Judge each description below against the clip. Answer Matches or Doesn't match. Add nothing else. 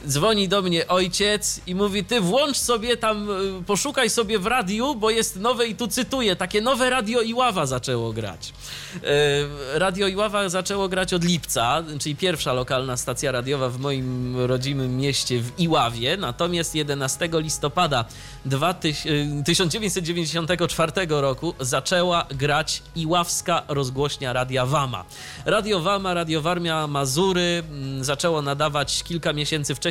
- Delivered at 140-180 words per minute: Doesn't match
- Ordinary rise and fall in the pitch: Doesn't match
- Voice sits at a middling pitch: Matches